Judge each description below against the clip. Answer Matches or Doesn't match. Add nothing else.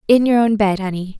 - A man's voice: Doesn't match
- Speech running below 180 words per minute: Doesn't match